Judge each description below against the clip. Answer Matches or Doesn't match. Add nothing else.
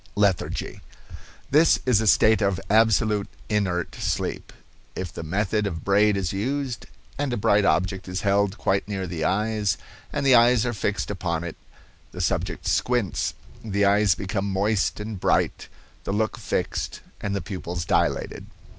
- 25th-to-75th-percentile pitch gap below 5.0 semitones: Matches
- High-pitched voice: Doesn't match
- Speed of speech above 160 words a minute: Doesn't match